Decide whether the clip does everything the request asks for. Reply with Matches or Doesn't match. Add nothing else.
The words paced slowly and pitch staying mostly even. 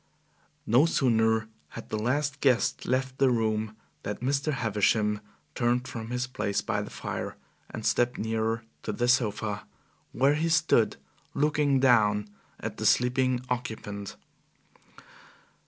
Doesn't match